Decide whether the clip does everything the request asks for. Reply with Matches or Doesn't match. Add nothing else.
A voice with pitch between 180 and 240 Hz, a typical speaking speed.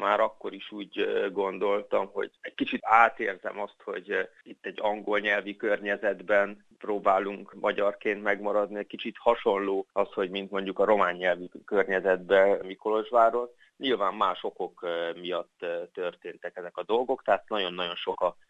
Doesn't match